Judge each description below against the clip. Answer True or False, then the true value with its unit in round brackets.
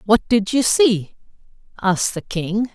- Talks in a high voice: True (210 Hz)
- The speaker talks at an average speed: True (155 wpm)